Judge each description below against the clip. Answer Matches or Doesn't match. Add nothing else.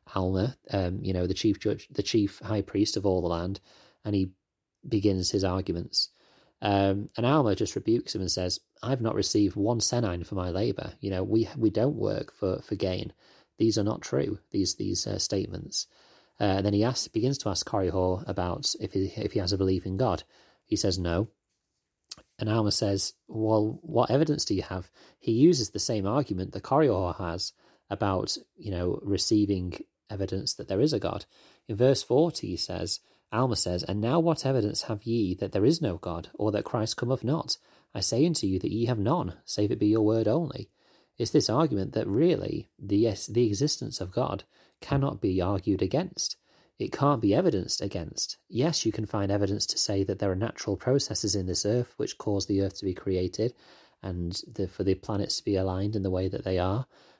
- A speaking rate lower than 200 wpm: Doesn't match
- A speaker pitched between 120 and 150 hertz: Doesn't match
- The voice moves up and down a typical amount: Matches